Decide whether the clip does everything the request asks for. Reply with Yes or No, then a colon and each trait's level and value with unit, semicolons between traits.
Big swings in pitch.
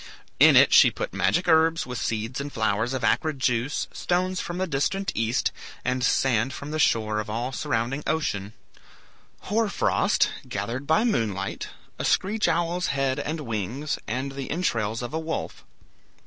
Yes: wide, 6.0 semitones